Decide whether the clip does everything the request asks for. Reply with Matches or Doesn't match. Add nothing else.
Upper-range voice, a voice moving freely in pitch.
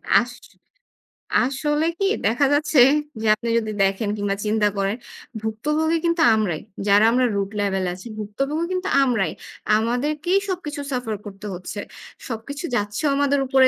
Matches